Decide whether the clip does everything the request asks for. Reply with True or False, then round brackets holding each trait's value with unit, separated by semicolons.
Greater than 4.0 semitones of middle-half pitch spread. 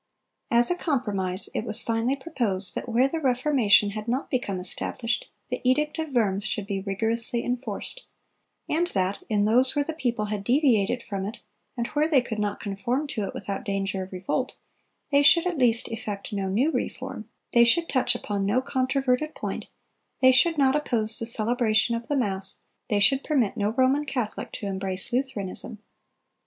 True (4.5 semitones)